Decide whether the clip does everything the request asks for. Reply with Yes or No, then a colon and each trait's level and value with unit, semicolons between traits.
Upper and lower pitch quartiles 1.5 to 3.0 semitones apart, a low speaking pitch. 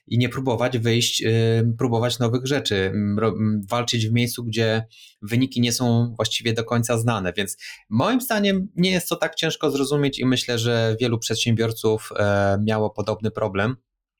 Yes: narrow, 2.4 semitones; low, 115 Hz